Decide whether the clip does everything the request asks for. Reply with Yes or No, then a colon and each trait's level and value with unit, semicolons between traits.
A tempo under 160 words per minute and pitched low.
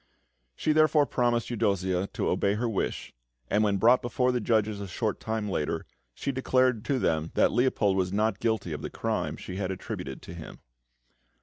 No: average, 185 wpm; low, 110 Hz